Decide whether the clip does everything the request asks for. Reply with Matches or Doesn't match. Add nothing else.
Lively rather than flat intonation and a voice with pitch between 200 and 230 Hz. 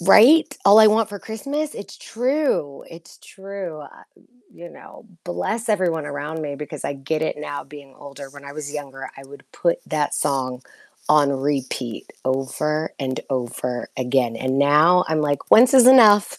Doesn't match